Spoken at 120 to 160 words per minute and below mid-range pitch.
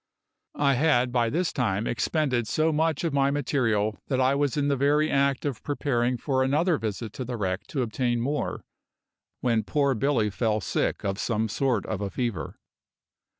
No: average, 180 wpm; low, 130 Hz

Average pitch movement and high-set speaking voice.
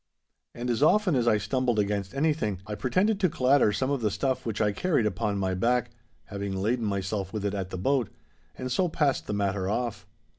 No: average, 4.7 semitones; low, 110 Hz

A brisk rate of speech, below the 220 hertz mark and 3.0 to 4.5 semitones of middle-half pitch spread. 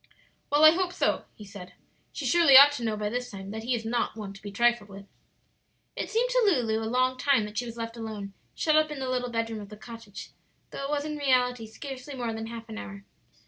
No: fast, 245 wpm; high, 235 Hz; average, 4.2 semitones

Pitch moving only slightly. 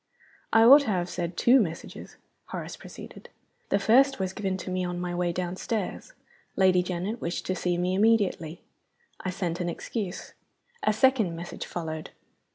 No: average, 3.4 semitones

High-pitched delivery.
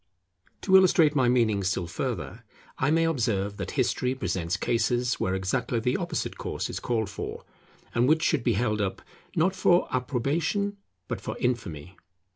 No: low, 120 Hz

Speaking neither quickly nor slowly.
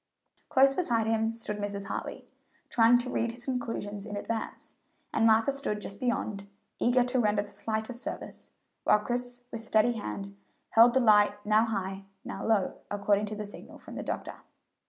Yes: average, 175 wpm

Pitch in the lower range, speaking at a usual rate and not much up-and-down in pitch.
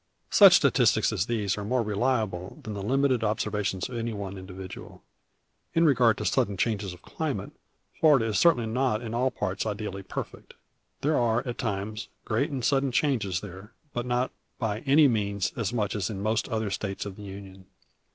No: low, 110 Hz; average, 185 wpm; average, 3.6 semitones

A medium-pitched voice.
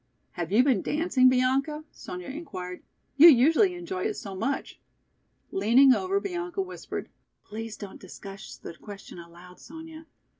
No: very high, 260 Hz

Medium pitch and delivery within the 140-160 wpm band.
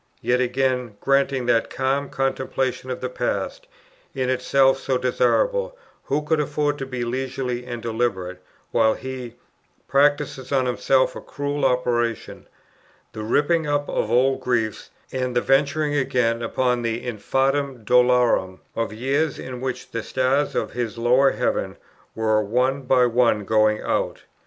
No: low, 125 Hz; average, 145 wpm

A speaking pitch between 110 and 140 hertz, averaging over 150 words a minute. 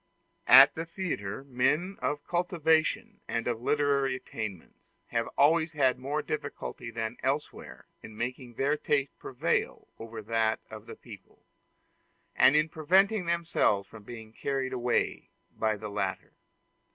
No: low, 135 Hz; slow, 135 wpm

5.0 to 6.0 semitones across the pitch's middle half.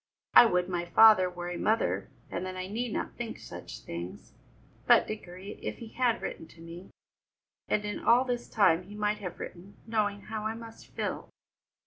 No: average, 3.8 semitones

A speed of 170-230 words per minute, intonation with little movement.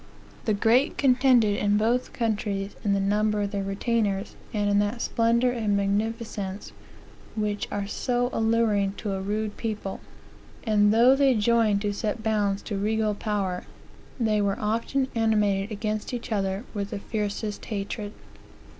No: average, 150 wpm; narrow, 2.1 semitones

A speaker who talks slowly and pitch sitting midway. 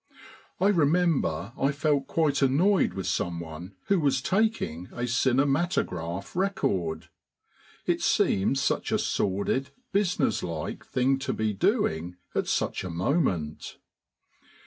No: slow, 120 wpm; low, 130 Hz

